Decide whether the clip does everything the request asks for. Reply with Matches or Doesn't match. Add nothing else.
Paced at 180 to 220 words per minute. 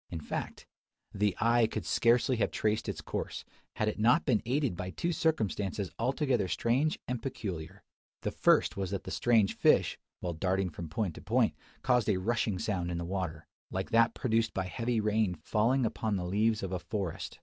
Matches